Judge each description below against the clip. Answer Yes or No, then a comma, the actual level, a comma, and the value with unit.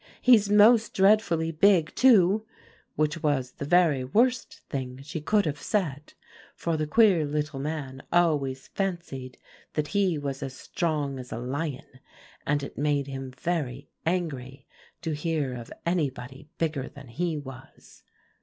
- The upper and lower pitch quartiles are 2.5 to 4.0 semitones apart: No, average, 4.5 semitones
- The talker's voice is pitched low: No, medium, 150 Hz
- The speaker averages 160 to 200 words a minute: No, average, 145 wpm